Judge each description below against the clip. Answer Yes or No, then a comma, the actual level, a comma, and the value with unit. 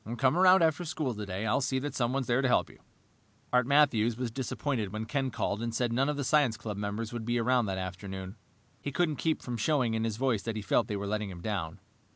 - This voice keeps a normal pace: No, fast, 245 wpm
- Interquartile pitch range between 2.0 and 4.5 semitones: Yes, average, 4.2 semitones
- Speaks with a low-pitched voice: Yes, low, 120 Hz